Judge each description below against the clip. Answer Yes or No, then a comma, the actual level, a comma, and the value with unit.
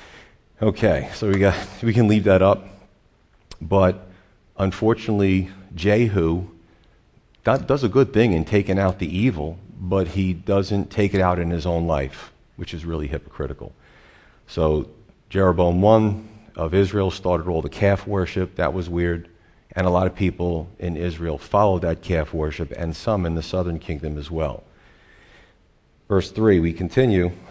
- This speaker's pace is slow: No, average, 155 wpm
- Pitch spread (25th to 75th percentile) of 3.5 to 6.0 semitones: No, average, 2.9 semitones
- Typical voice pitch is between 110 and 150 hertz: No, very low, 90 Hz